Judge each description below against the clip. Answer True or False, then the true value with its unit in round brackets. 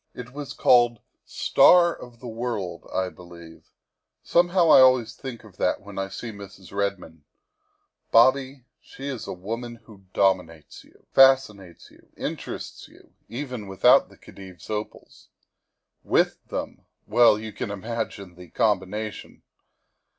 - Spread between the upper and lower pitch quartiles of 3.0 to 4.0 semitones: False (4.6 semitones)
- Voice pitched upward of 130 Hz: False (110 Hz)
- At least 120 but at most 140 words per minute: True (135 wpm)